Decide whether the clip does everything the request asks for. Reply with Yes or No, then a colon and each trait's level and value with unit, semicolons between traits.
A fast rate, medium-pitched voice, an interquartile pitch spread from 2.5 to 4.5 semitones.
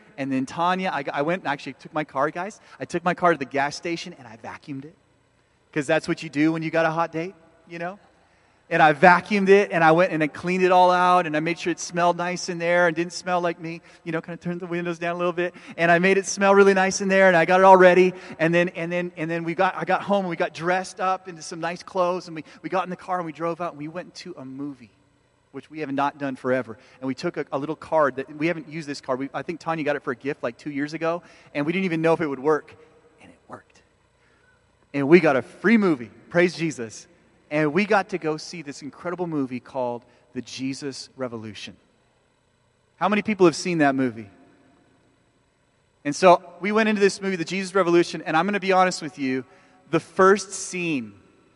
Yes: fast, 255 wpm; medium, 170 Hz; average, 4.0 semitones